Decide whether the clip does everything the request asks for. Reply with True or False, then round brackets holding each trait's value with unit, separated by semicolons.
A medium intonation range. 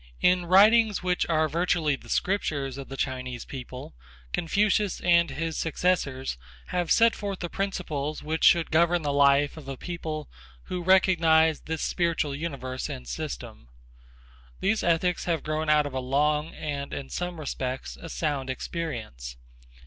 True (4.1 semitones)